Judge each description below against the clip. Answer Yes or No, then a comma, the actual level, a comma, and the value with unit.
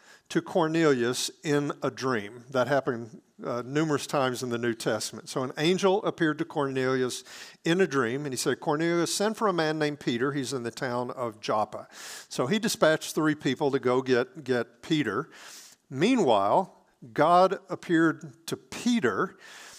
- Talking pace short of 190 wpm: Yes, average, 165 wpm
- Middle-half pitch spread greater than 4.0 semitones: Yes, average, 4.4 semitones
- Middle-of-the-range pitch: Yes, medium, 145 Hz